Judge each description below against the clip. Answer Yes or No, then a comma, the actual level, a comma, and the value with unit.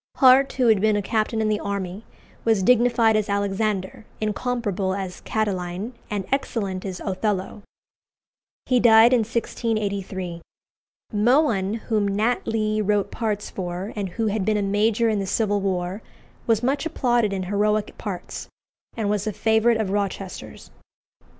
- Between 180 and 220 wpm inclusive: No, average, 150 wpm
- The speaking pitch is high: Yes, high, 210 Hz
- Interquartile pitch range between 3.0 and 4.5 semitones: No, narrow, 2.4 semitones